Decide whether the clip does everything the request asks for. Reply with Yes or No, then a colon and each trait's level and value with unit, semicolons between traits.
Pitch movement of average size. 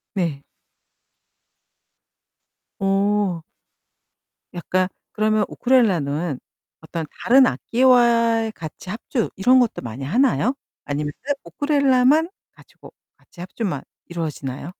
No: wide, 6.9 semitones